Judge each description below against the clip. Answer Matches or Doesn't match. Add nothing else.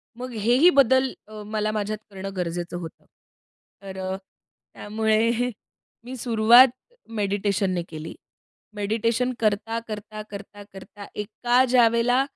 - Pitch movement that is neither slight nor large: Matches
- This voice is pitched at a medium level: Doesn't match